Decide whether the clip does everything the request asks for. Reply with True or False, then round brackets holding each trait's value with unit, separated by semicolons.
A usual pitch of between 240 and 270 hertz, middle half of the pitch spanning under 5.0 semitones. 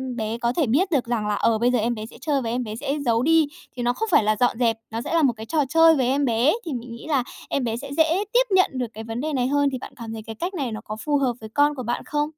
True (250 Hz; 4.4 semitones)